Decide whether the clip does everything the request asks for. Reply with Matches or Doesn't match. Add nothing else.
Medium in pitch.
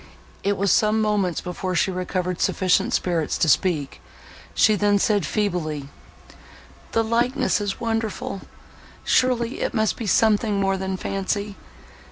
Doesn't match